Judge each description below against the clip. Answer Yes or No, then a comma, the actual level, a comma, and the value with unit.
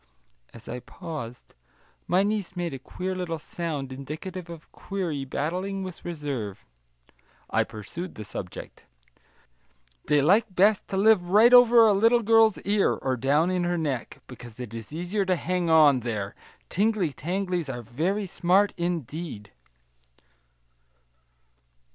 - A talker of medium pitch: Yes, medium, 170 Hz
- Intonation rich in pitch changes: Yes, wide, 6.1 semitones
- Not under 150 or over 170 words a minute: No, slow, 135 wpm